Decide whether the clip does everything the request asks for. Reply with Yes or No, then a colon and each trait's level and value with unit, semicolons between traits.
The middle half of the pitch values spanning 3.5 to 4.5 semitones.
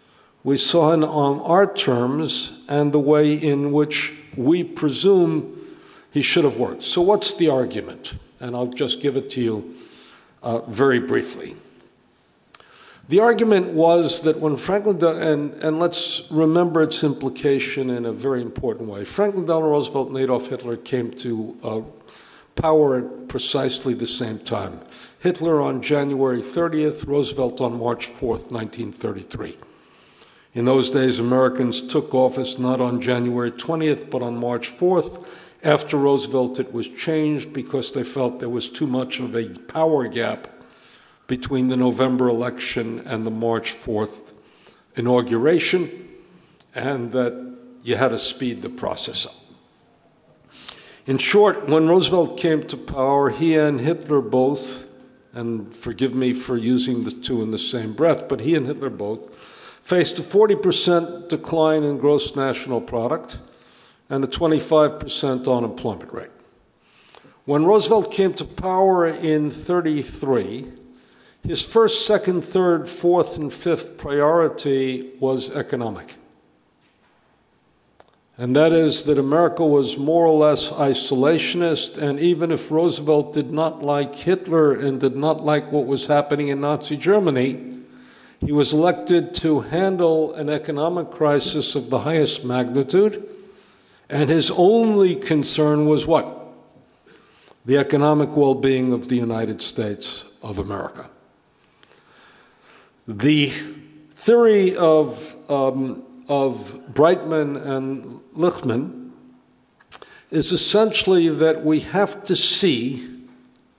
Yes: average, 4.2 semitones